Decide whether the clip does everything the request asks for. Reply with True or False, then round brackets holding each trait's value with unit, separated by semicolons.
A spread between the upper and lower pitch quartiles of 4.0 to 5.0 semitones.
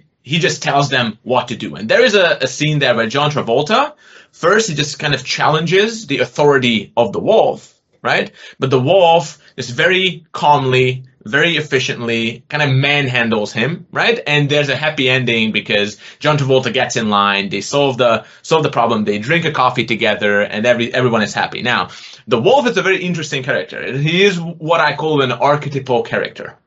True (4.6 semitones)